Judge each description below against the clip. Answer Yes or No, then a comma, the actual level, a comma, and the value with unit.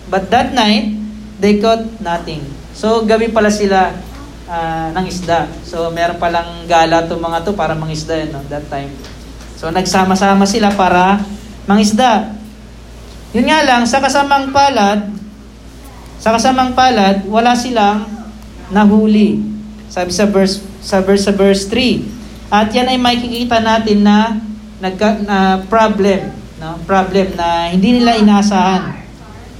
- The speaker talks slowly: No, average, 140 wpm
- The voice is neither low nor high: No, high, 200 Hz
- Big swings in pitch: No, average, 3.6 semitones